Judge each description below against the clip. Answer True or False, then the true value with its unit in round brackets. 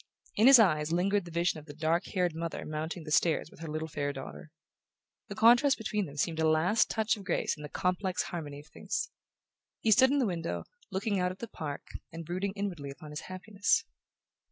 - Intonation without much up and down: False (4.4 semitones)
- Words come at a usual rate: False (210 wpm)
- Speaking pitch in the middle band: True (175 Hz)